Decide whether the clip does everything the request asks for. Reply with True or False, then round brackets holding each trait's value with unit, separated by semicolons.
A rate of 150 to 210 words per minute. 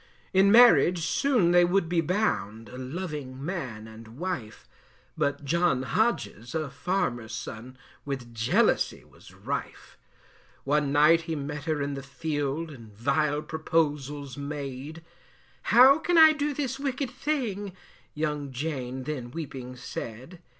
False (135 wpm)